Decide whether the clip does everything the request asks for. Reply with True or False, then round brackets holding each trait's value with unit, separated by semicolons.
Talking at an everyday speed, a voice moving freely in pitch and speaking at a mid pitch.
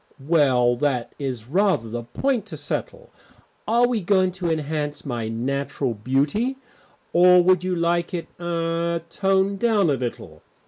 True (145 wpm; 5.9 semitones; 170 Hz)